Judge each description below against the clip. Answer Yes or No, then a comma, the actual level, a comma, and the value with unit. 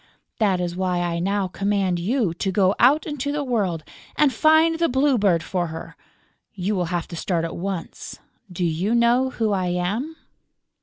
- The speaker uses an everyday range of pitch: No, wide, 5.8 semitones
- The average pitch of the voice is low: No, high, 195 Hz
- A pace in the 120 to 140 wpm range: No, average, 185 wpm